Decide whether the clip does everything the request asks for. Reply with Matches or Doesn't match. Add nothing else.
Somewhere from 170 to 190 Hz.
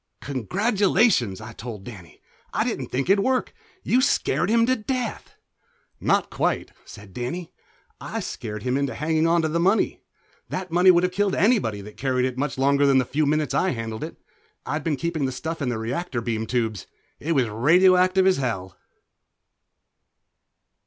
Doesn't match